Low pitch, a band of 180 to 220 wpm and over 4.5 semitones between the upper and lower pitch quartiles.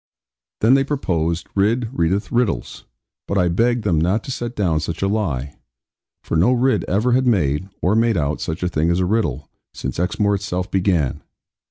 Yes: very low, 95 Hz; average, 185 wpm; wide, 5.4 semitones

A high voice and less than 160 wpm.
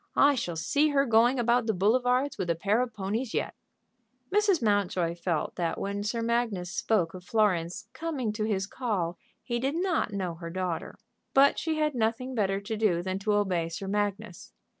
No: high, 210 Hz; average, 185 wpm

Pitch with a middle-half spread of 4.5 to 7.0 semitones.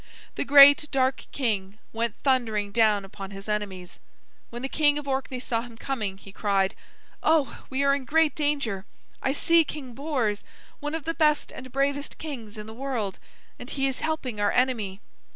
Yes: average, 5.2 semitones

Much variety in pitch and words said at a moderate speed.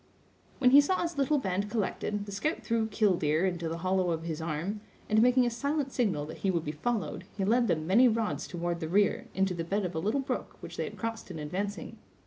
No: wide, 5.7 semitones; fast, 235 wpm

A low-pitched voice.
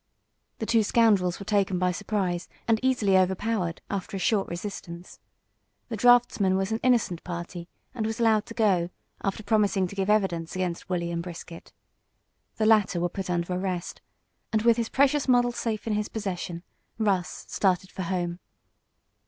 No: high, 195 Hz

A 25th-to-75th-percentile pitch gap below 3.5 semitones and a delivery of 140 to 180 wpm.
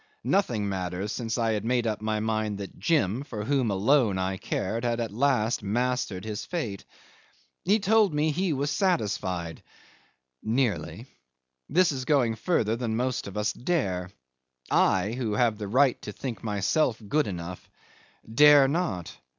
No: wide, 5.5 semitones; average, 160 wpm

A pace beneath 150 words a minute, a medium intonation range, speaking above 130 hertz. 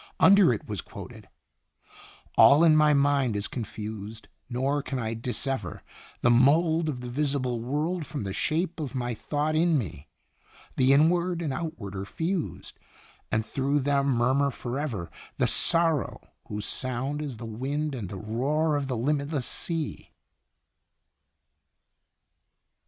Yes: average, 140 wpm; average, 4.3 semitones; medium, 140 Hz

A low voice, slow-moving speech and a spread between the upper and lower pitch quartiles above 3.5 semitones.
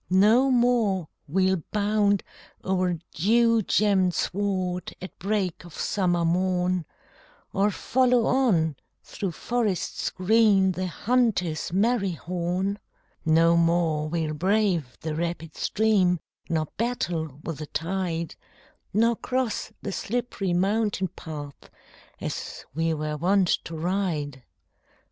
No: medium, 185 Hz; slow, 110 wpm; average, 3.9 semitones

